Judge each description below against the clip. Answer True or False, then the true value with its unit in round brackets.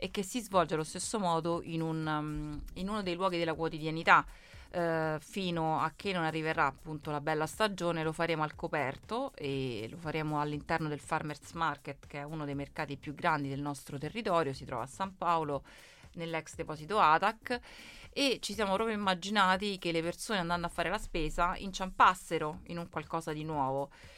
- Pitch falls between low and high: True (165 Hz)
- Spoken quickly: True (180 wpm)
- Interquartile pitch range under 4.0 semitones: True (3.4 semitones)